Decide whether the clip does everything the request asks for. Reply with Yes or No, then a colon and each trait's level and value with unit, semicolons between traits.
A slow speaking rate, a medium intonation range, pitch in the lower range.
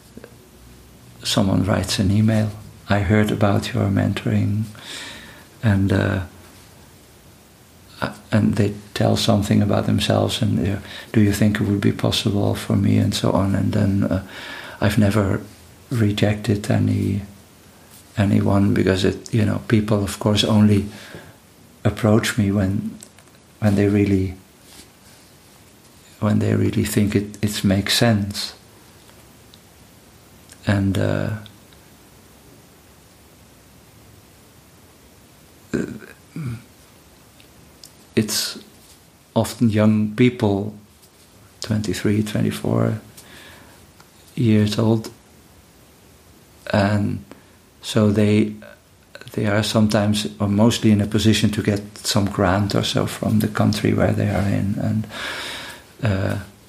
No: slow, 100 wpm; narrow, 1.8 semitones; low, 105 Hz